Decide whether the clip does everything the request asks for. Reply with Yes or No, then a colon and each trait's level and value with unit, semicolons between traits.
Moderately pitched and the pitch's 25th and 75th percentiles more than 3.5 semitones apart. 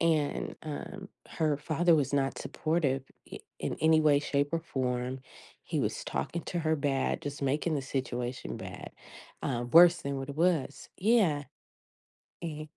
No: medium, 150 Hz; average, 3.2 semitones